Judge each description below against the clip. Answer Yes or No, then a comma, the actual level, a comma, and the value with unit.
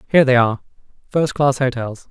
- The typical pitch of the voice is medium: No, low, 130 Hz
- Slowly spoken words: Yes, slow, 115 wpm